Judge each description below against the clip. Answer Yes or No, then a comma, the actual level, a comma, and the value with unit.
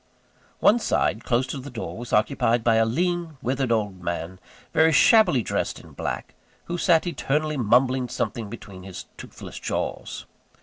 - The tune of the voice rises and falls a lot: Yes, wide, 5.8 semitones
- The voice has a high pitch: No, low, 125 Hz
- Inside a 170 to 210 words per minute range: No, average, 160 wpm